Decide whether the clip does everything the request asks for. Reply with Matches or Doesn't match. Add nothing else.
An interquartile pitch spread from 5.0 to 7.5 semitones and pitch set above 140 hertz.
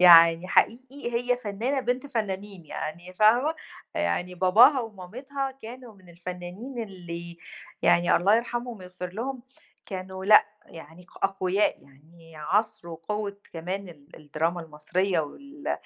Matches